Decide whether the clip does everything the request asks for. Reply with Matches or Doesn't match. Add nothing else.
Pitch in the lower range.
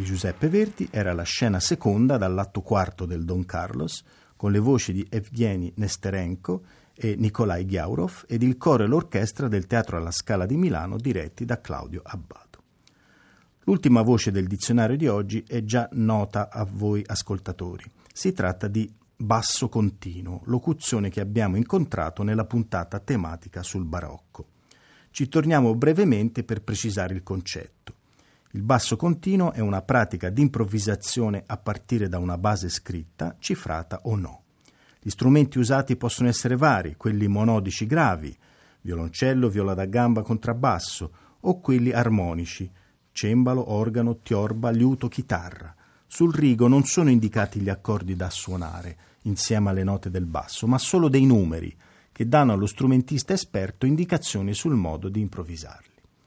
Matches